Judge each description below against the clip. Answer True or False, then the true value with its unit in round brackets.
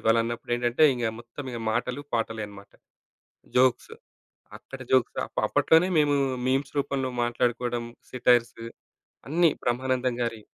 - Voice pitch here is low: True (120 Hz)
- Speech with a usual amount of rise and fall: False (2.0 semitones)